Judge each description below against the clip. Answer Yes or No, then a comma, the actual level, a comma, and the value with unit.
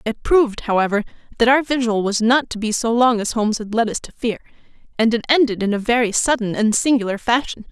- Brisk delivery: Yes, fast, 225 wpm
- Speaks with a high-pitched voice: Yes, high, 230 Hz